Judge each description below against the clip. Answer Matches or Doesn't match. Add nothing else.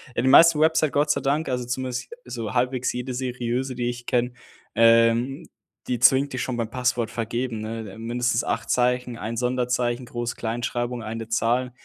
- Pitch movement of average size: Doesn't match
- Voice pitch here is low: Matches